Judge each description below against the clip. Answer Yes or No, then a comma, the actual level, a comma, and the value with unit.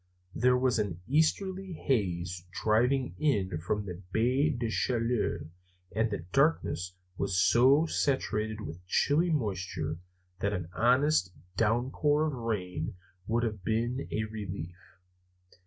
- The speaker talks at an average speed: No, slow, 125 wpm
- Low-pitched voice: Yes, low, 110 Hz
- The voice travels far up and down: Yes, wide, 6.0 semitones